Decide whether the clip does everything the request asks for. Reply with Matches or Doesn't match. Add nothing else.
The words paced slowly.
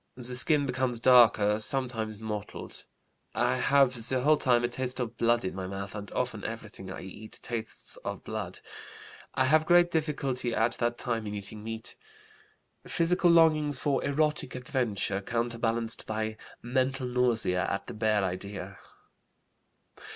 Doesn't match